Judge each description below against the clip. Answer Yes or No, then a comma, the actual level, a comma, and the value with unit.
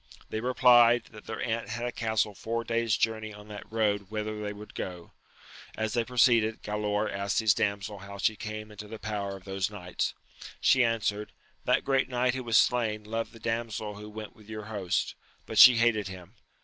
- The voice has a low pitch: Yes, low, 110 Hz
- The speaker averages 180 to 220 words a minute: Yes, average, 195 wpm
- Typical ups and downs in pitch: No, narrow, 1.9 semitones